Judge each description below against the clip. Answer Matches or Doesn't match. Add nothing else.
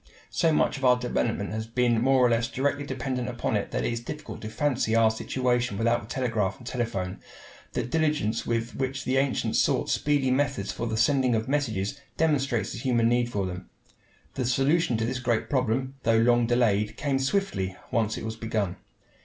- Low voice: Matches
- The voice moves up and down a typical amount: Matches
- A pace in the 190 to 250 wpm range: Matches